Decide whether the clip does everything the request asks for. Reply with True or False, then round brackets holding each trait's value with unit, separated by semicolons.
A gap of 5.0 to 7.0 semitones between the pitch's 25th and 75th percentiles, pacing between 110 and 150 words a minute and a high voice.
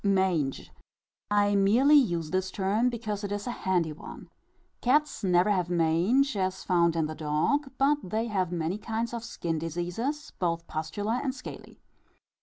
False (5.4 semitones; 160 wpm; 195 Hz)